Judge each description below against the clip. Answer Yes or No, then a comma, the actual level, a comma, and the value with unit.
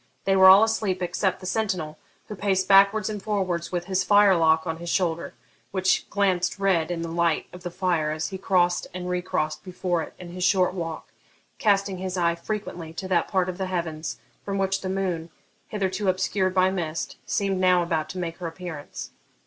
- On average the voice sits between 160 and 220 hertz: Yes, medium, 185 Hz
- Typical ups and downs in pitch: No, narrow, 2.2 semitones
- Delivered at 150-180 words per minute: No, average, 195 wpm